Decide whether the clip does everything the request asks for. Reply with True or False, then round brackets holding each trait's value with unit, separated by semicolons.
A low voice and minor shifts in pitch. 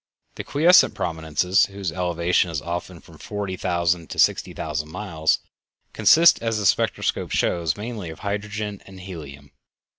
False (90 Hz; 4.1 semitones)